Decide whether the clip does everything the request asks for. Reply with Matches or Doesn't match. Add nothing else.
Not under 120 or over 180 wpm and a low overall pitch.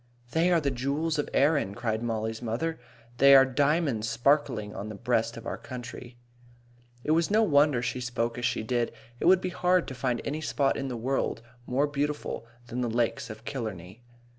Doesn't match